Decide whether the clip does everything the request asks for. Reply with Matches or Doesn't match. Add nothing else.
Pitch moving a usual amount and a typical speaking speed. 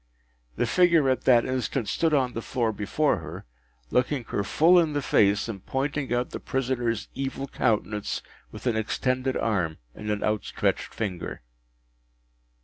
Matches